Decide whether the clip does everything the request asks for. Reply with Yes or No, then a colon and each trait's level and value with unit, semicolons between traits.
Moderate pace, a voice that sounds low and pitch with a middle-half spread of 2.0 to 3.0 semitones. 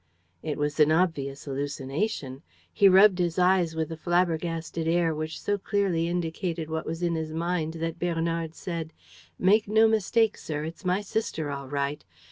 No: average, 165 wpm; medium, 165 Hz; narrow, 2.6 semitones